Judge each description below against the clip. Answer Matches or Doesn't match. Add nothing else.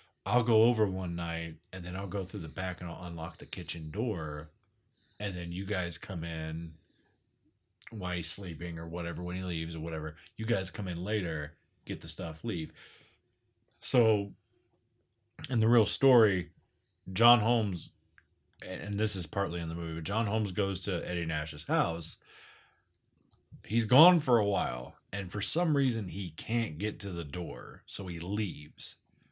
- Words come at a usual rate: Matches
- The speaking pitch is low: Matches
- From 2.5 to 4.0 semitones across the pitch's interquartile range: Doesn't match